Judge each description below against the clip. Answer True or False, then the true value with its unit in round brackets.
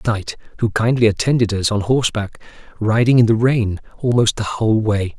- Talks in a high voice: False (110 Hz)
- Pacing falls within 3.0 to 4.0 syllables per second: False (5.5 syllables/s)